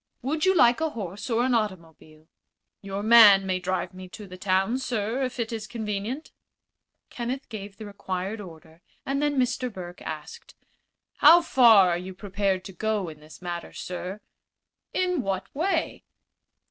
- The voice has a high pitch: Yes, high, 205 Hz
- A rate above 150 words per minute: Yes, average, 160 wpm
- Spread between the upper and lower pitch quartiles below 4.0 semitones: No, average, 4.8 semitones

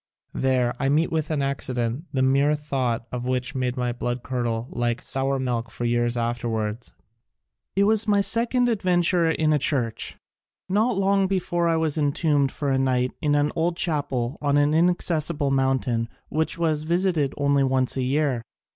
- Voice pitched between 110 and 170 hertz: Yes, medium, 140 Hz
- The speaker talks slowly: No, average, 175 wpm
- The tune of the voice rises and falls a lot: No, average, 4.5 semitones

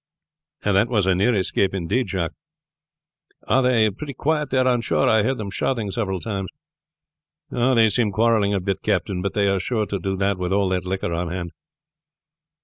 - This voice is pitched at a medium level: No, low, 100 Hz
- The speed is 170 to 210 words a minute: Yes, average, 185 wpm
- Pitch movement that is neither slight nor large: Yes, average, 3.6 semitones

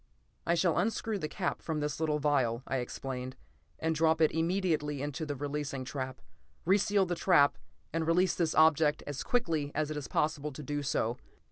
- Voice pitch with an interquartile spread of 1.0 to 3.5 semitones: Yes, narrow, 2.6 semitones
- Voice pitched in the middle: Yes, medium, 150 Hz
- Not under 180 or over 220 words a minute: Yes, average, 190 wpm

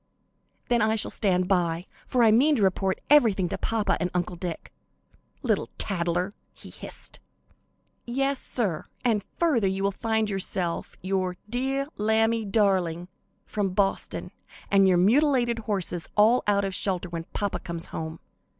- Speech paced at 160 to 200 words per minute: No, average, 150 wpm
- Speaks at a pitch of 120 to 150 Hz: No, high, 200 Hz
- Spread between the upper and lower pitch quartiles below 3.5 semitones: No, average, 3.9 semitones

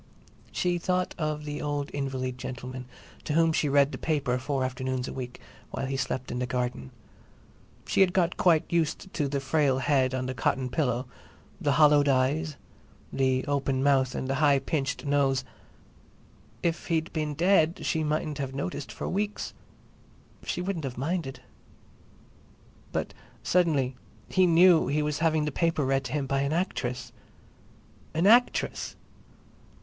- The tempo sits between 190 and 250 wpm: No, average, 155 wpm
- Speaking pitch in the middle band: Yes, medium, 145 Hz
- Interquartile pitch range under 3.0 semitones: No, average, 3.5 semitones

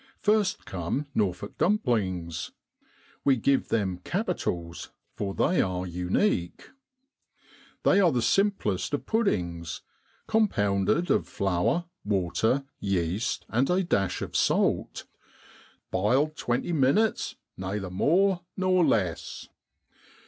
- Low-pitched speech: Yes, low, 110 Hz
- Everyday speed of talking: No, slow, 105 wpm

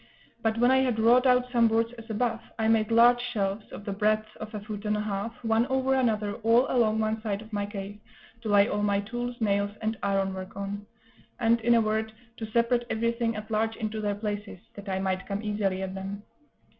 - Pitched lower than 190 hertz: No, high, 215 Hz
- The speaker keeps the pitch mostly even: Yes, narrow, 2.2 semitones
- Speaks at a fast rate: Yes, fast, 220 wpm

